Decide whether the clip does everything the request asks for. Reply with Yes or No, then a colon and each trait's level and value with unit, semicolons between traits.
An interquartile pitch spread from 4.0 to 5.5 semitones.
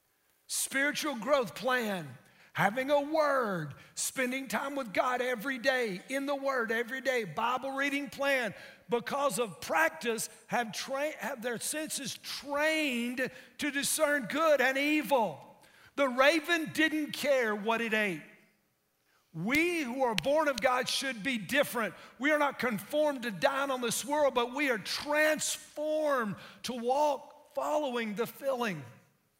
No: average, 3.6 semitones